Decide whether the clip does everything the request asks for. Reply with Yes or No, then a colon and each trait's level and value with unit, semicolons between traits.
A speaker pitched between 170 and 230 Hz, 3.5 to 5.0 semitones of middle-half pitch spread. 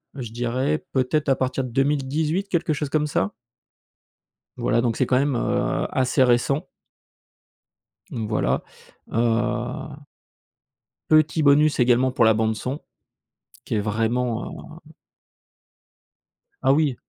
No: low, 130 Hz; average, 4.0 semitones